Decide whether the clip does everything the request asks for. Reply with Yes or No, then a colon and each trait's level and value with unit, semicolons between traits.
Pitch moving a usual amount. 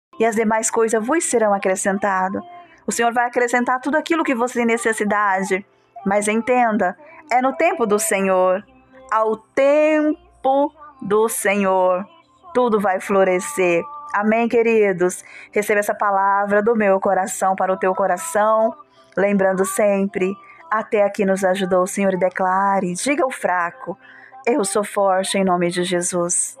Yes: average, 4.1 semitones